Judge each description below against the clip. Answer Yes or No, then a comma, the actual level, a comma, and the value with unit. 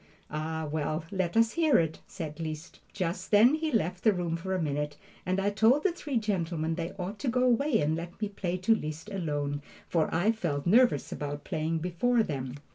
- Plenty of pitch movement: Yes, wide, 5.7 semitones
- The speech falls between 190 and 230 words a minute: Yes, average, 200 wpm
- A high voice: No, medium, 175 Hz